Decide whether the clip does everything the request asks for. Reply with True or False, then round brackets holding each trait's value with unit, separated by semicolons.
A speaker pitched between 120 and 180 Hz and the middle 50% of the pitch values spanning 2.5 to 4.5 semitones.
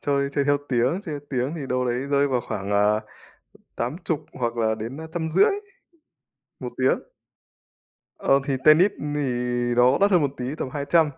True (140 Hz; 3.8 semitones)